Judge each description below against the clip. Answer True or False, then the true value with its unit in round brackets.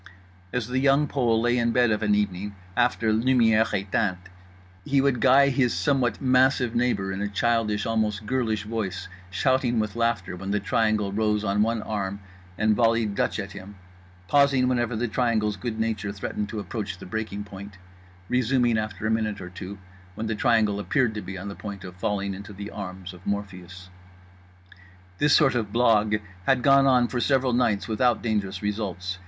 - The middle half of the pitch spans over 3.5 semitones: False (3.2 semitones)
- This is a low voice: True (110 Hz)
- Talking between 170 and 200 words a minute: True (180 wpm)